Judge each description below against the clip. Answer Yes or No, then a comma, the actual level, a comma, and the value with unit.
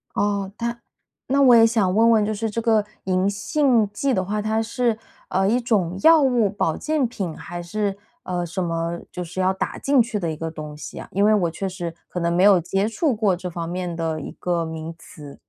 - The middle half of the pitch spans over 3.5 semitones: Yes, average, 4.5 semitones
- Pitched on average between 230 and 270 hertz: No, high, 195 Hz